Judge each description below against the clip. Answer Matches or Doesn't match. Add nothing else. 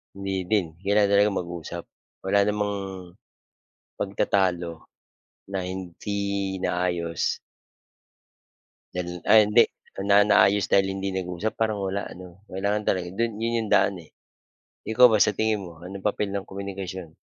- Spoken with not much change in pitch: Matches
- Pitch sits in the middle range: Doesn't match